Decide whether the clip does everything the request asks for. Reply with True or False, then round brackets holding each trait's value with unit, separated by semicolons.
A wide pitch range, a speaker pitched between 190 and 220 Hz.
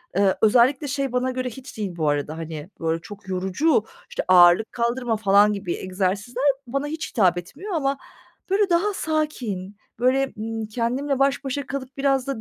False (6.3 semitones; 235 Hz)